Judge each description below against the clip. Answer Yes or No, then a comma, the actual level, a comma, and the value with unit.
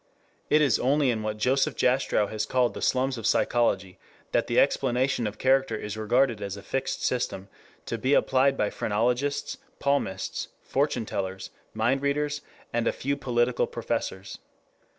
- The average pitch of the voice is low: Yes, low, 125 Hz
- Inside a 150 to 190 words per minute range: Yes, average, 155 wpm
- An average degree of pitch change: Yes, average, 4.0 semitones